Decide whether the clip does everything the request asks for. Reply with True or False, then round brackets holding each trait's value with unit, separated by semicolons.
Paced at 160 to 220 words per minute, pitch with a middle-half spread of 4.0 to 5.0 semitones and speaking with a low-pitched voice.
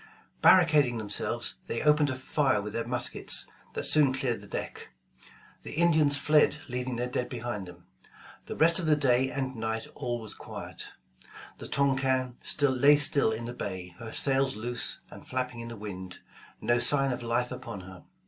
False (175 wpm; 3.6 semitones; 125 Hz)